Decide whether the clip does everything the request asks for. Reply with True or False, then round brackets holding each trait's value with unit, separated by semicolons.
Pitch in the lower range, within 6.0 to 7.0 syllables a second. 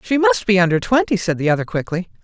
False (185 Hz; 6.5 syllables/s)